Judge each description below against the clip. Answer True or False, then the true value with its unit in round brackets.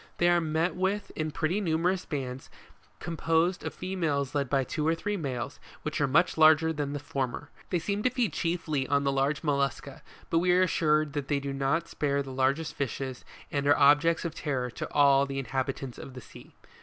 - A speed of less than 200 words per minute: False (205 wpm)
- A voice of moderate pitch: True (150 Hz)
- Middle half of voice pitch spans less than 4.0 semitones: True (3.2 semitones)